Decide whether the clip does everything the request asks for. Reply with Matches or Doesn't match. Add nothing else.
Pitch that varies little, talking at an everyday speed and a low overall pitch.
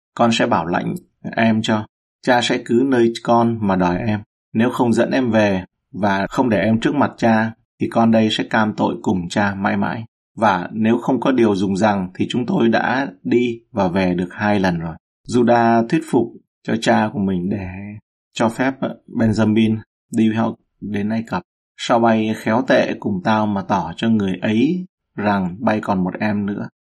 Matches